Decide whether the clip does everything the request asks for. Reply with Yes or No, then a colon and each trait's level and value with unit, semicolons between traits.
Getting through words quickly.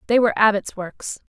No: average, 185 wpm